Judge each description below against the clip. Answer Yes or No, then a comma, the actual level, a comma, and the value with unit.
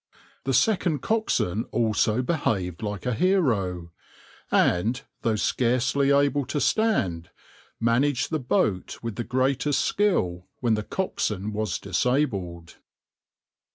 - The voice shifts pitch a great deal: Yes, wide, 6.2 semitones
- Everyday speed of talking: No, slow, 115 wpm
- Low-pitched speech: Yes, low, 120 Hz